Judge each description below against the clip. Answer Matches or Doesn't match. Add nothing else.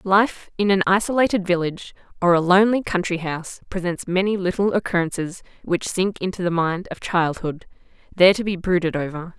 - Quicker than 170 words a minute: Doesn't match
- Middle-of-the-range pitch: Matches